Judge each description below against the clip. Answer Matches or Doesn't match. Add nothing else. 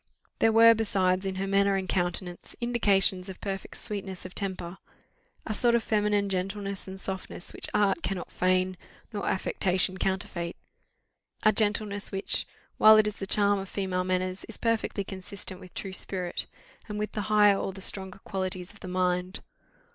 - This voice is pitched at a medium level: Doesn't match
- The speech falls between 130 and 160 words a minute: Doesn't match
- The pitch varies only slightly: Matches